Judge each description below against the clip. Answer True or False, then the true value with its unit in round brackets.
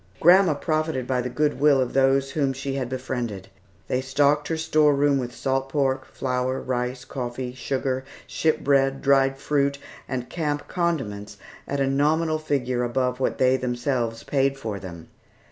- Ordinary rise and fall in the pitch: False (2.2 semitones)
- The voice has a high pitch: False (135 Hz)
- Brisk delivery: False (160 wpm)